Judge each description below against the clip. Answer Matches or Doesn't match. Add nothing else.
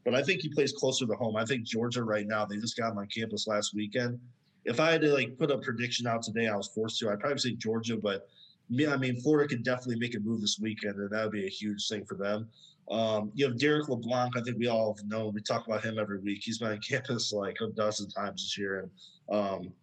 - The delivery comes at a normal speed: Doesn't match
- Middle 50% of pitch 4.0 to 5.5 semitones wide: Doesn't match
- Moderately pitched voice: Doesn't match